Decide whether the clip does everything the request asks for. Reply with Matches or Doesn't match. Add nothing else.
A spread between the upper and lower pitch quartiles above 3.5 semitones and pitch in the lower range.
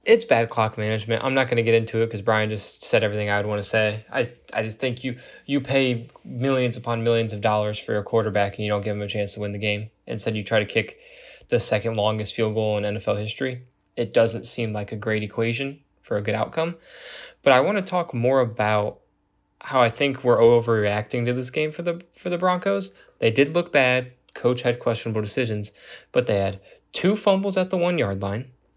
Matches